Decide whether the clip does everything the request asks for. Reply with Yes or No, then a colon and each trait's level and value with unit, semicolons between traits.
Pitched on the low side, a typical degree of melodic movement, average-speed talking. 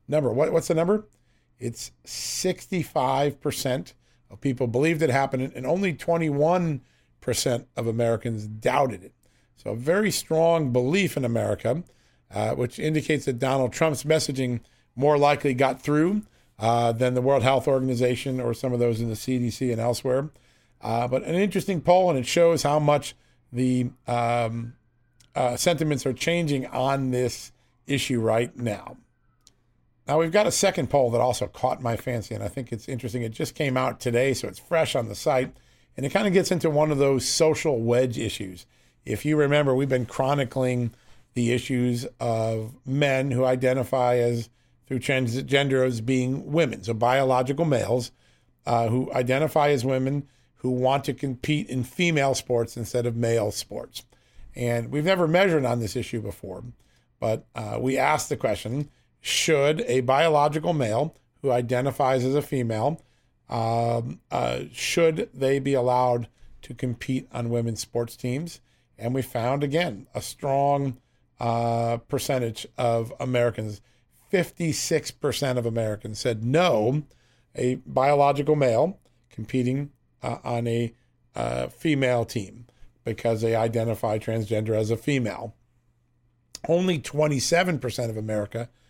Yes: low, 125 Hz; average, 3.3 semitones; average, 150 wpm